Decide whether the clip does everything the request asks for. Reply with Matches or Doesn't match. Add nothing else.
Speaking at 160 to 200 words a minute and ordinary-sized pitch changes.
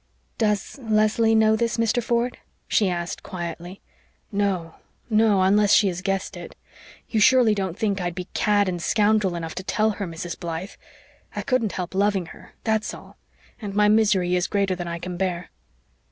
Matches